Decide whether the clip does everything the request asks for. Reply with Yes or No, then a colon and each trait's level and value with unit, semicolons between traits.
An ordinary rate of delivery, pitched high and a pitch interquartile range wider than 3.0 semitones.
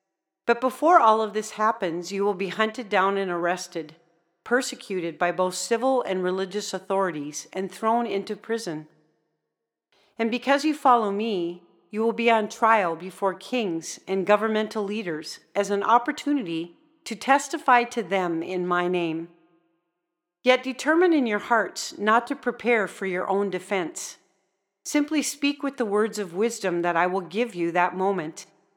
Yes: average, 155 wpm; high, 200 Hz; average, 5.0 semitones